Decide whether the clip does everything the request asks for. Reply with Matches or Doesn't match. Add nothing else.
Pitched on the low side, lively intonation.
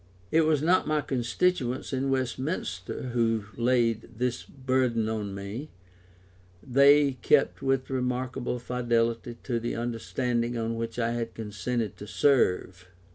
Doesn't match